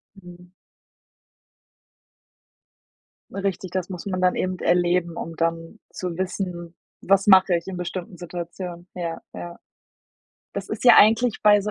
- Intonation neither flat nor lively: No, narrow, 1.9 semitones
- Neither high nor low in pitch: Yes, medium, 180 Hz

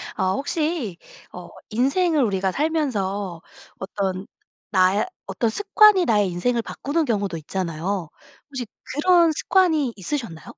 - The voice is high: Yes, high, 220 Hz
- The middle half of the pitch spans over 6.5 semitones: Yes, wide, 8.3 semitones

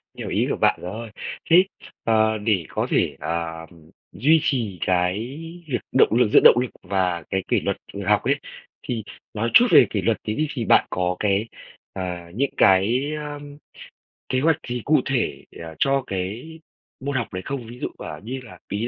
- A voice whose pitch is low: Yes, low, 110 Hz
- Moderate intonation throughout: No, wide, 5.7 semitones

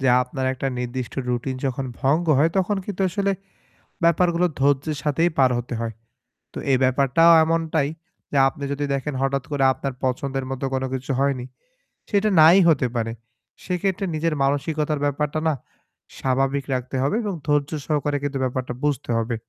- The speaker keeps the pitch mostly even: No, average, 3.3 semitones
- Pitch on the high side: No, medium, 140 Hz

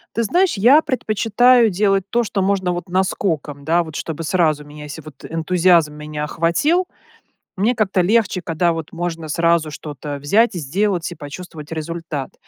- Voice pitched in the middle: Yes, medium, 170 Hz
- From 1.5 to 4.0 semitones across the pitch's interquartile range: No, average, 4.6 semitones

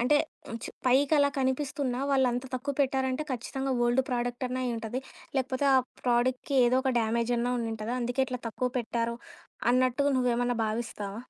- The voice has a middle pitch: No, very high, 250 Hz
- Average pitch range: No, narrow, 1.8 semitones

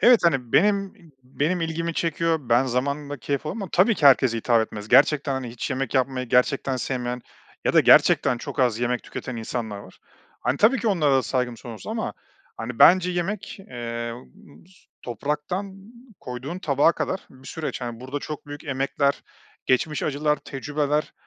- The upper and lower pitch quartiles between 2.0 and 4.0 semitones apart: No, average, 4.7 semitones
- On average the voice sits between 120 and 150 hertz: Yes, medium, 140 Hz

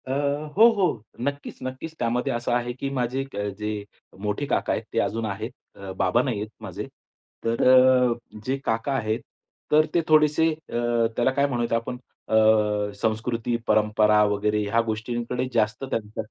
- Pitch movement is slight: No, average, 3.6 semitones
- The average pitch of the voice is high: No, low, 120 Hz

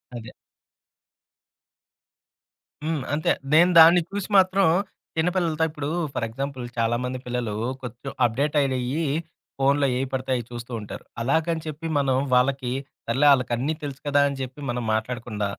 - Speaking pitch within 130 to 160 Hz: Yes, low, 135 Hz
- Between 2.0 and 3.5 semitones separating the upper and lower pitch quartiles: No, average, 4.0 semitones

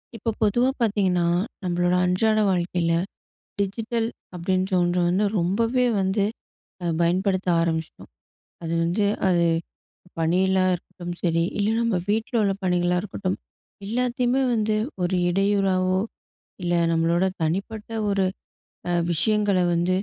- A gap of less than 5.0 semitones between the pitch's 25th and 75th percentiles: Yes, average, 3.2 semitones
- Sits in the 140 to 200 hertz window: Yes, high, 190 Hz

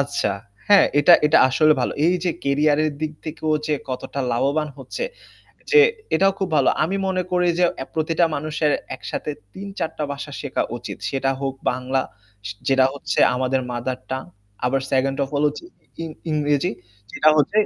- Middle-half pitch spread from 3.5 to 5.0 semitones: No, average, 2.9 semitones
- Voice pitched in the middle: Yes, medium, 145 Hz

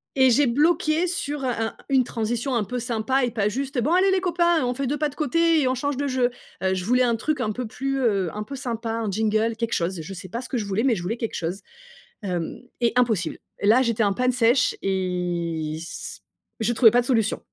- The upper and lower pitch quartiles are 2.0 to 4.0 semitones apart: No, average, 4.4 semitones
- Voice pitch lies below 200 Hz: No, high, 240 Hz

